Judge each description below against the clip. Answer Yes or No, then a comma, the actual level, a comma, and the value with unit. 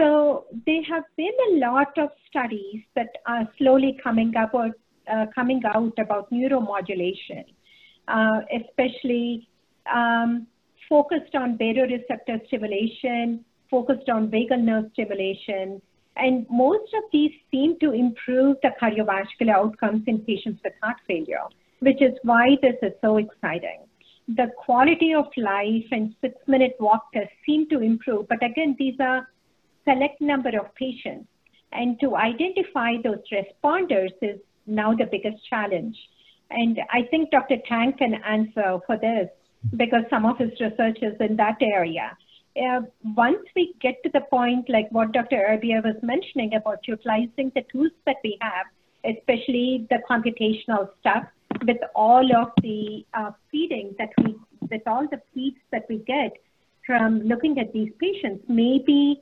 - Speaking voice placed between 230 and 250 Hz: Yes, high, 240 Hz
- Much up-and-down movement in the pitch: No, average, 3.6 semitones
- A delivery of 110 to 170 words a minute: Yes, average, 150 wpm